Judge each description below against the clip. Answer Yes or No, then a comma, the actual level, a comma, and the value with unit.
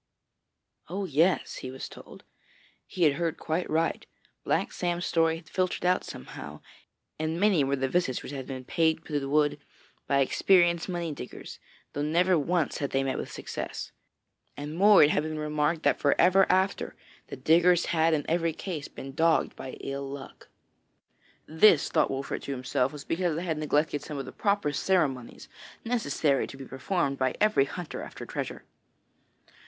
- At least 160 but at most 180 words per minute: Yes, average, 175 wpm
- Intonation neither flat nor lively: Yes, average, 3.9 semitones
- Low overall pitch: No, medium, 155 Hz